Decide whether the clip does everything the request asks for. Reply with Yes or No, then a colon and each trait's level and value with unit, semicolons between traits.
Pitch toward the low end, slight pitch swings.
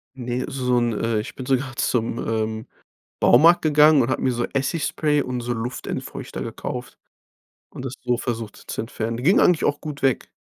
No: low, 125 Hz; average, 3.4 semitones